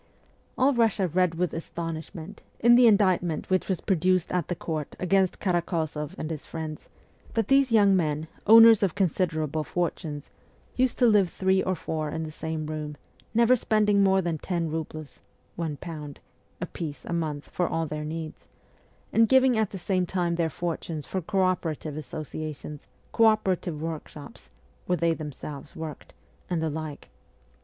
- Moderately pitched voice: Yes, medium, 170 Hz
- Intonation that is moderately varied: Yes, average, 3.7 semitones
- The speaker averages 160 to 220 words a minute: Yes, average, 165 wpm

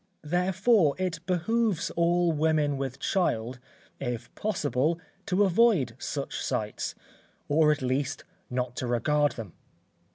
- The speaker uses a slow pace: Yes, slow, 120 wpm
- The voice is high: No, medium, 150 Hz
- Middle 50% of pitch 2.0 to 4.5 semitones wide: No, wide, 5.6 semitones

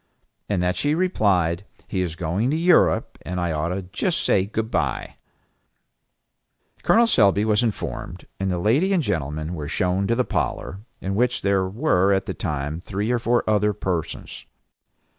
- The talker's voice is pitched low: Yes, low, 100 Hz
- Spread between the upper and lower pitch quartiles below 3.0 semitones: No, average, 4.6 semitones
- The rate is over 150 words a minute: Yes, average, 165 wpm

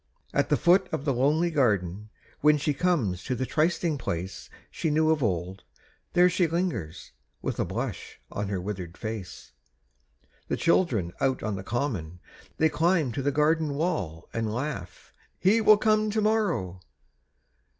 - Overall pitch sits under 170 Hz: Yes, medium, 140 Hz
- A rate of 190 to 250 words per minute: No, average, 160 wpm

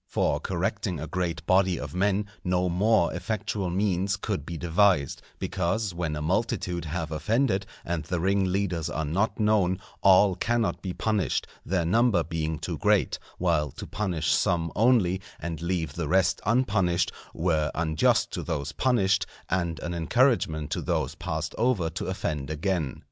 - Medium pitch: No, very low, 90 Hz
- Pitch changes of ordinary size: Yes, average, 3.6 semitones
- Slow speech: No, average, 155 wpm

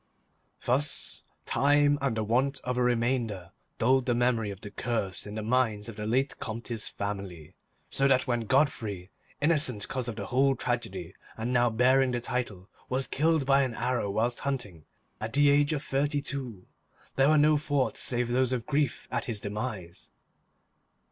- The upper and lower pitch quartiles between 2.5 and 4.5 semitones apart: Yes, average, 3.9 semitones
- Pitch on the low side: Yes, low, 125 Hz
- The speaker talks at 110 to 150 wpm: No, average, 175 wpm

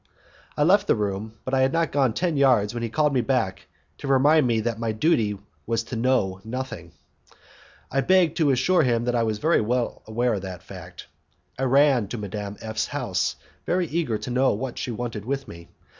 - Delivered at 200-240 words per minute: Yes, fast, 205 wpm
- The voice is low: Yes, low, 120 Hz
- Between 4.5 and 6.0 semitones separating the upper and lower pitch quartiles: No, average, 4.0 semitones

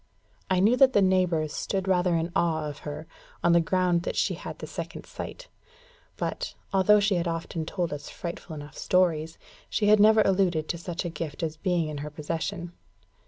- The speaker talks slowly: No, average, 190 wpm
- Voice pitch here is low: No, medium, 175 Hz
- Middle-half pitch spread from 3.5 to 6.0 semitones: No, average, 3.0 semitones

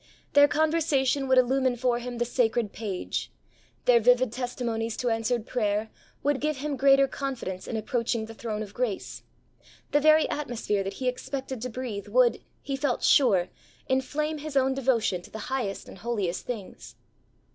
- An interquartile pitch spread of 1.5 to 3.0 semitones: No, average, 3.4 semitones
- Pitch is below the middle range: No, high, 245 Hz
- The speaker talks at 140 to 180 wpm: Yes, average, 165 wpm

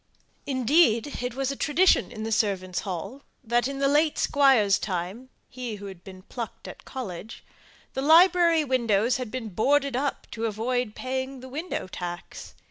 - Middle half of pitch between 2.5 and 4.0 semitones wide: No, average, 4.6 semitones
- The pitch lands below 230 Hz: No, very high, 250 Hz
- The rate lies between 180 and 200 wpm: No, average, 165 wpm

